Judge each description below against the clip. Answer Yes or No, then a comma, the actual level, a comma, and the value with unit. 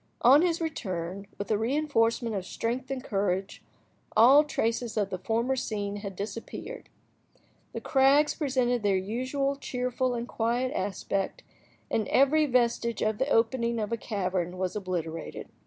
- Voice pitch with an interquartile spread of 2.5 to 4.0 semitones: No, average, 4.5 semitones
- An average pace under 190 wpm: Yes, average, 145 wpm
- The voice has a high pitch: Yes, high, 230 Hz